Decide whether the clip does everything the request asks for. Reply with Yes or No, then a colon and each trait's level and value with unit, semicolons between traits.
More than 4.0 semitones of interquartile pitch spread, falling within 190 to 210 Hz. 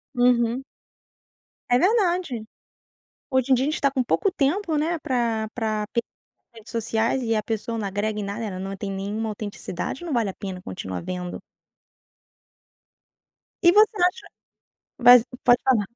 No: average, 4.5 semitones; high, 235 Hz